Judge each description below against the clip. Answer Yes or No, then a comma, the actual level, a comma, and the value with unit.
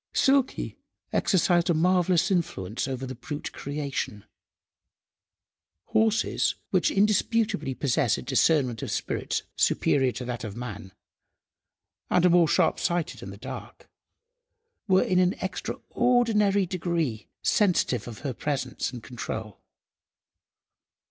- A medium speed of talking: No, slow, 115 wpm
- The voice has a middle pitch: Yes, medium, 160 Hz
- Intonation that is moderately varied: No, wide, 7.1 semitones